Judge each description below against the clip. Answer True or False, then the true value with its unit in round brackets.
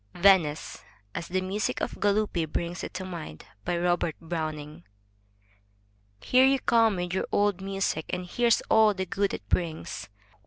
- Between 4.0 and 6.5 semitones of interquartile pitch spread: False (3.1 semitones)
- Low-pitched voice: False (185 Hz)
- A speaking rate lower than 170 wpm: True (150 wpm)